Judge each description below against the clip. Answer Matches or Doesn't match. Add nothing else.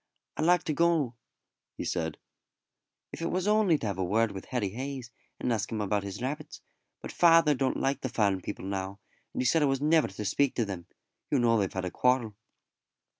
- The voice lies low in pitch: Matches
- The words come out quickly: Matches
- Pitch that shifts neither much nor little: Doesn't match